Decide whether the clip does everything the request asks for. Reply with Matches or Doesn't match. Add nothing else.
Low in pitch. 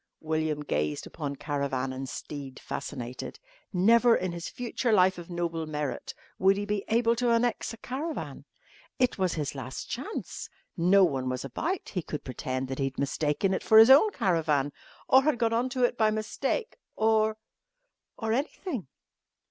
Doesn't match